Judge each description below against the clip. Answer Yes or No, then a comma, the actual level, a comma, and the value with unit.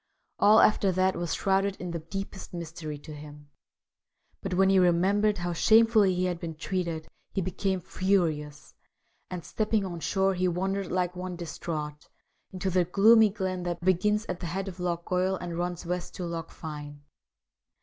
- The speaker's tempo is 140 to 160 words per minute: No, average, 170 wpm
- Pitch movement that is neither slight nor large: No, narrow, 2.3 semitones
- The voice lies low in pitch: No, medium, 180 Hz